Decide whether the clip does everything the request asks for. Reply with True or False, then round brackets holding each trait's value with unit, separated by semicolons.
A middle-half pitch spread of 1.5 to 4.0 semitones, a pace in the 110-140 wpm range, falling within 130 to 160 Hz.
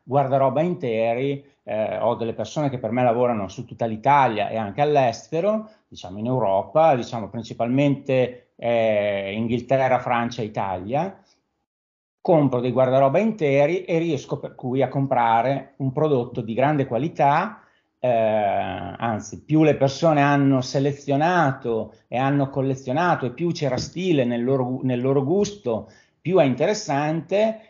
True (3.6 semitones; 135 wpm; 135 Hz)